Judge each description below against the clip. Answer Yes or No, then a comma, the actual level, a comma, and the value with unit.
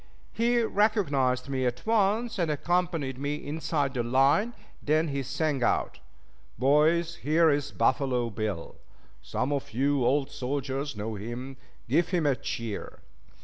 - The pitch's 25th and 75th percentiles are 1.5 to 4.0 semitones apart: No, average, 4.5 semitones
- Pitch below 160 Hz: Yes, medium, 140 Hz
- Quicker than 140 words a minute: No, slow, 135 wpm